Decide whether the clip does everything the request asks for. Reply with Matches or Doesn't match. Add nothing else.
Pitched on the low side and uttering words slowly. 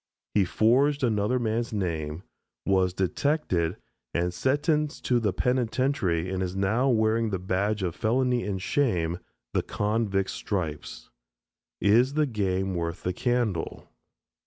Matches